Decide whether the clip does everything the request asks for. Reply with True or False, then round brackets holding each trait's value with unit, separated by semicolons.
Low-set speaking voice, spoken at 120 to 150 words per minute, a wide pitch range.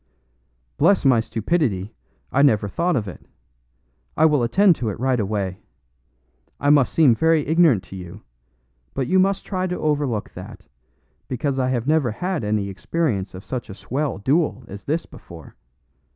False (130 Hz; 165 wpm; 7.2 semitones)